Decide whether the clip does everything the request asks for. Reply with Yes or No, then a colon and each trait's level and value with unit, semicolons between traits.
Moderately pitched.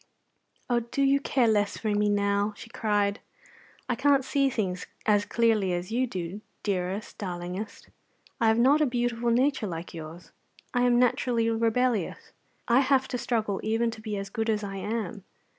No: high, 220 Hz